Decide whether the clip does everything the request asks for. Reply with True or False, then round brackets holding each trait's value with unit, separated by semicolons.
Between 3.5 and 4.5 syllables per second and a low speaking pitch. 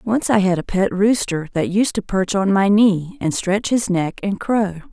False (4.3 syllables/s; 195 Hz)